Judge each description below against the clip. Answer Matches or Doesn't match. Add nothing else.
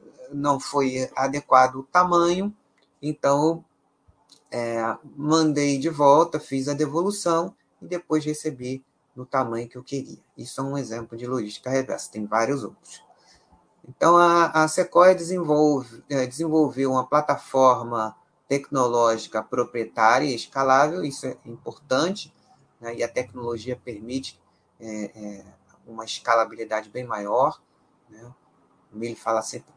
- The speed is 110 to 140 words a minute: Matches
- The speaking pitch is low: Matches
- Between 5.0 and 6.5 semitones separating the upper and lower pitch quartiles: Doesn't match